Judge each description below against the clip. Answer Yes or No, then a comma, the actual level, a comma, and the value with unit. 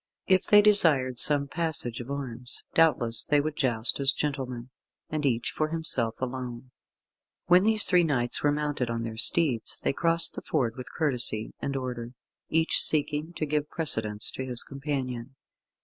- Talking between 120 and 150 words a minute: No, average, 165 wpm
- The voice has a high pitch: No, low, 135 Hz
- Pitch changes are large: No, average, 4.2 semitones